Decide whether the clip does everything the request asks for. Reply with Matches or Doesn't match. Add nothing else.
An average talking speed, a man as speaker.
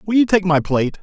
Doesn't match